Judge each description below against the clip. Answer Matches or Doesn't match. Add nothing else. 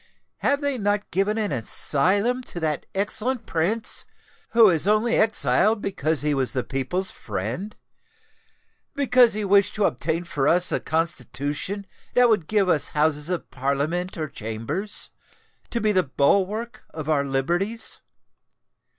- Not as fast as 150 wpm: Matches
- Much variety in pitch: Matches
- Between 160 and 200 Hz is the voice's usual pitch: Matches